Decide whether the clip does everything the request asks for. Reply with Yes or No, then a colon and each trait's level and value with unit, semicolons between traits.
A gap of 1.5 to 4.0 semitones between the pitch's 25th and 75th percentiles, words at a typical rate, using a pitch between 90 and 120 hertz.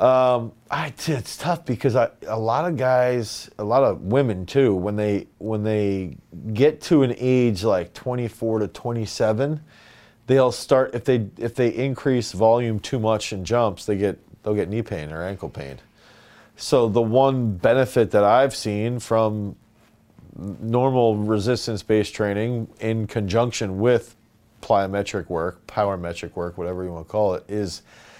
Yes: average, 3.1 semitones; average, 160 wpm; low, 110 Hz